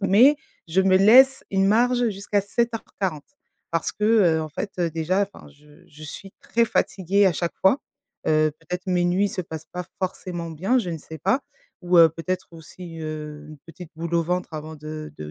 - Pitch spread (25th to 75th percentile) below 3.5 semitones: No, average, 3.8 semitones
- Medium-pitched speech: Yes, medium, 180 Hz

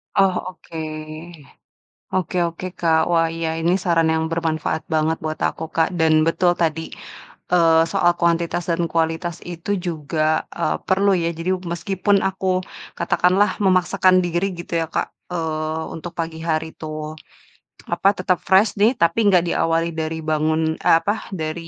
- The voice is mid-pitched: Yes, medium, 165 Hz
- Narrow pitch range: Yes, narrow, 1.9 semitones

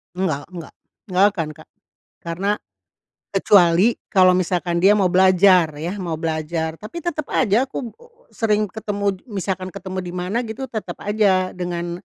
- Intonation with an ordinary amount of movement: Yes, average, 3.0 semitones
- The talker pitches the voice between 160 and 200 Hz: Yes, medium, 185 Hz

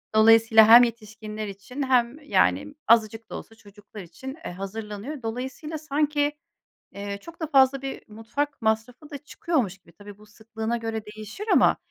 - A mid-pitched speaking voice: No, high, 225 Hz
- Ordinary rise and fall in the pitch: Yes, average, 4.3 semitones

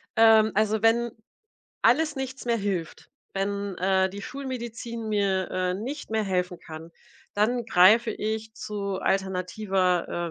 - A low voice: No, high, 210 Hz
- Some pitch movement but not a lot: Yes, average, 3.3 semitones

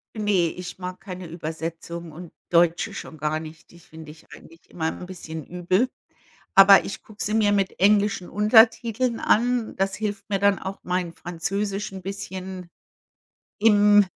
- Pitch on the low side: No, high, 190 Hz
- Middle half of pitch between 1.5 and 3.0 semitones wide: No, average, 3.4 semitones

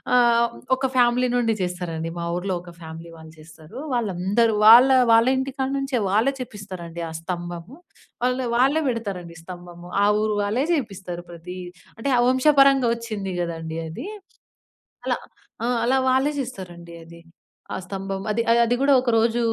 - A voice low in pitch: No, high, 210 Hz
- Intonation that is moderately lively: No, wide, 6.2 semitones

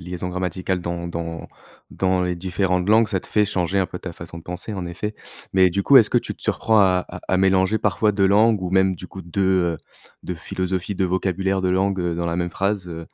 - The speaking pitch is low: Yes, very low, 95 Hz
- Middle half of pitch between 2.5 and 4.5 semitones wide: No, narrow, 1.8 semitones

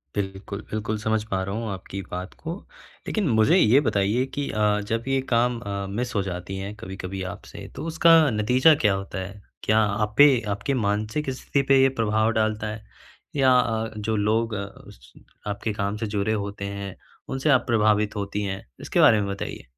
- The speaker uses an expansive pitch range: No, average, 2.8 semitones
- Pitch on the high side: No, low, 105 Hz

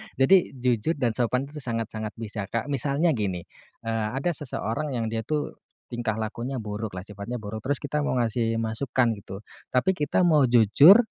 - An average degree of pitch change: Yes, average, 4.2 semitones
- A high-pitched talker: No, low, 120 Hz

